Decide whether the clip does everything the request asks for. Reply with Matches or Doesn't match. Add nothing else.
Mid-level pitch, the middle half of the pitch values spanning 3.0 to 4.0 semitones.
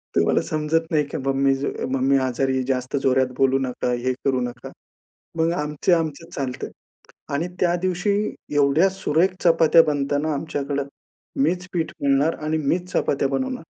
Matches